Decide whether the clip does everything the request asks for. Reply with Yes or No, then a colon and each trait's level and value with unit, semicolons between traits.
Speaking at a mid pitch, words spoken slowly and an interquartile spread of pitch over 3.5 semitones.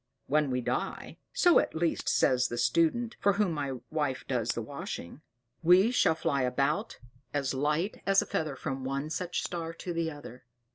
No: medium, 150 Hz; average, 185 wpm; average, 4.4 semitones